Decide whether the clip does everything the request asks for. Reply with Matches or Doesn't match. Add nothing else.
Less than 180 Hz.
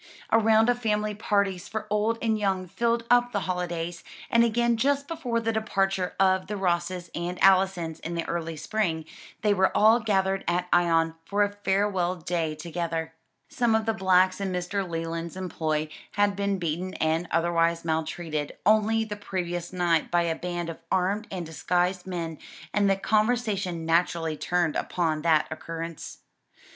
Doesn't match